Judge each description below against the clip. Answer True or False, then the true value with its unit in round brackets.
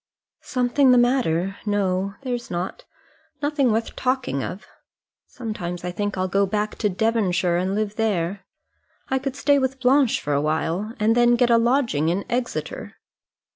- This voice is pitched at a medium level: False (215 Hz)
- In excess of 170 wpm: False (160 wpm)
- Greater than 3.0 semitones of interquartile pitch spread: True (5.2 semitones)